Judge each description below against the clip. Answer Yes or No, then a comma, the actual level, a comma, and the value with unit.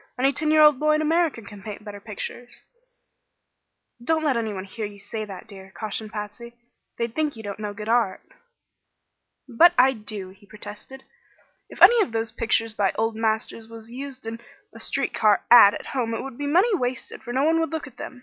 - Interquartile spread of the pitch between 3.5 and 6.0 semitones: Yes, average, 4.4 semitones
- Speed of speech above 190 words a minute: Yes, fast, 205 wpm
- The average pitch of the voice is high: Yes, high, 230 Hz